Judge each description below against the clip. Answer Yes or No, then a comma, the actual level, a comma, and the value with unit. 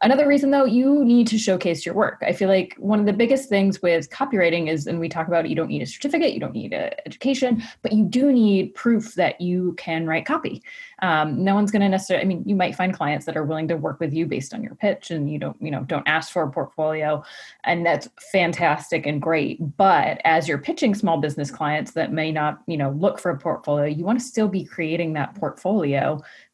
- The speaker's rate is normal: No, fast, 240 wpm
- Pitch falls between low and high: Yes, medium, 180 Hz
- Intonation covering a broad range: Yes, wide, 6.1 semitones